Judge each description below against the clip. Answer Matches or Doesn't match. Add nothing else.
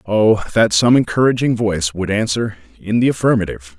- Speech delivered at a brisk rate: Doesn't match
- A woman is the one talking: Doesn't match